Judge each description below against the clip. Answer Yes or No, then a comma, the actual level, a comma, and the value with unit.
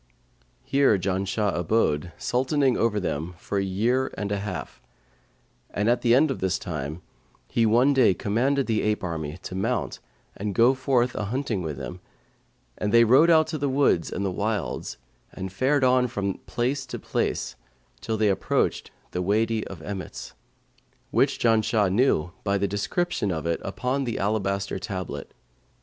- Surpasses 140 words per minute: Yes, average, 165 wpm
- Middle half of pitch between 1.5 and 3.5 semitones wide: No, average, 4.8 semitones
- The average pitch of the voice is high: No, low, 105 Hz